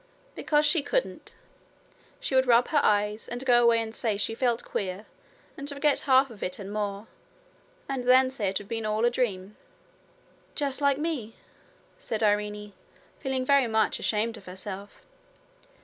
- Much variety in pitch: No, average, 4.1 semitones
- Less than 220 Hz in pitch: No, high, 230 Hz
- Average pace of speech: Yes, average, 165 wpm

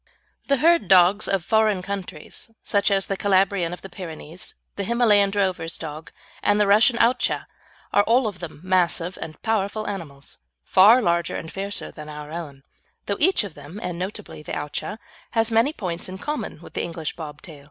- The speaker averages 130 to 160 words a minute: No, average, 185 wpm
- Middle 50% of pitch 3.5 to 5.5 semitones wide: Yes, average, 4.0 semitones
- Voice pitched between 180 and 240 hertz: Yes, high, 190 Hz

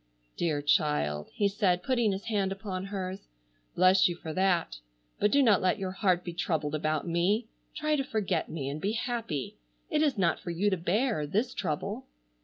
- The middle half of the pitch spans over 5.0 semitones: No, average, 4.2 semitones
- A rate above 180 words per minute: Yes, average, 190 wpm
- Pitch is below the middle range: No, medium, 185 Hz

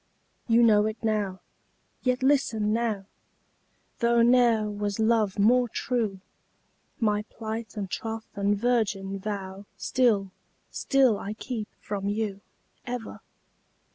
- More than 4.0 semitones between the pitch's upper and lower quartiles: No, narrow, 2.6 semitones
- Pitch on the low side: No, high, 220 Hz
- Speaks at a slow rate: Yes, slow, 115 wpm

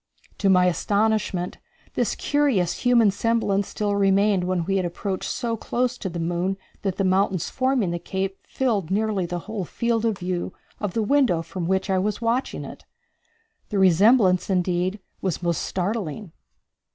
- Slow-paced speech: No, average, 165 wpm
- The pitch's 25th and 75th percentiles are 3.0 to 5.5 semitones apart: Yes, average, 3.3 semitones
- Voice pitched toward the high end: Yes, high, 195 Hz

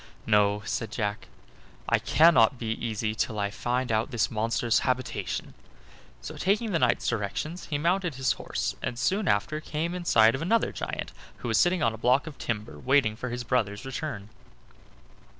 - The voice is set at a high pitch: No, low, 120 Hz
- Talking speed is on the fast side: No, average, 175 wpm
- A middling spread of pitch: No, wide, 5.7 semitones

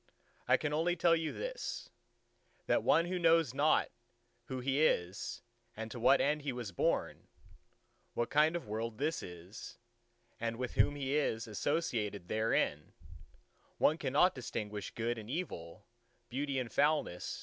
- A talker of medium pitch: No, low, 130 Hz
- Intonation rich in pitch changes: Yes, wide, 5.7 semitones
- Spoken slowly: No, average, 150 wpm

